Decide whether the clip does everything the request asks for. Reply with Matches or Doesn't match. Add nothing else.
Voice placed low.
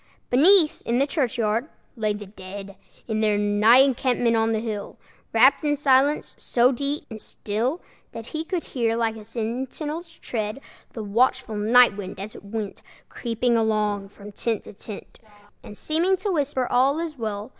Doesn't match